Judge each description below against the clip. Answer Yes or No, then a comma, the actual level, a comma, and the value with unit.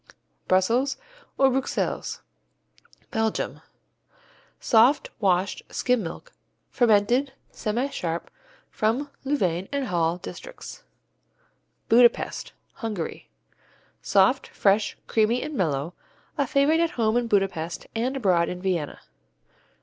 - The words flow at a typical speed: No, slow, 95 wpm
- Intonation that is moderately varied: No, wide, 6.2 semitones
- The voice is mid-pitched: No, high, 220 Hz